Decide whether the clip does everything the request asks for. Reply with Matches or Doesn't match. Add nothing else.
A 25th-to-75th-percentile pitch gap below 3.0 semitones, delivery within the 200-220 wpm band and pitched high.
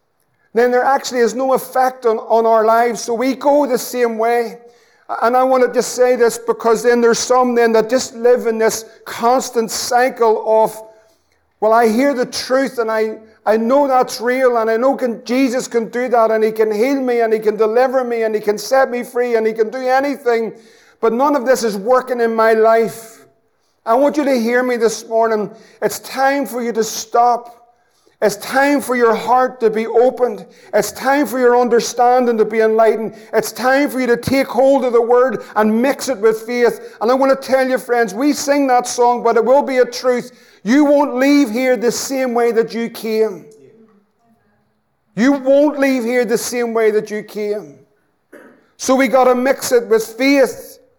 Matches